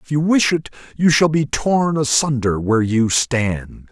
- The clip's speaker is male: Yes, male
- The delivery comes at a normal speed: Yes, average, 185 wpm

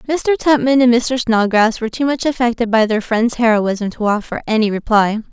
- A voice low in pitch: No, high, 230 Hz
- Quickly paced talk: No, average, 190 wpm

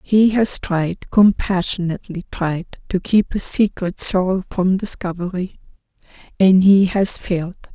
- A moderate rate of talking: No, slow, 125 wpm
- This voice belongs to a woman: Yes, female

